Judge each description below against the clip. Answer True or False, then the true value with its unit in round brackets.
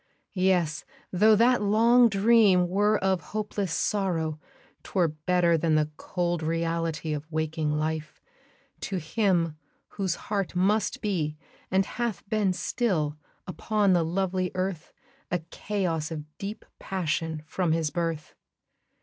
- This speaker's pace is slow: True (125 wpm)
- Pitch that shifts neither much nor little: True (4.0 semitones)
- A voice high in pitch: False (180 Hz)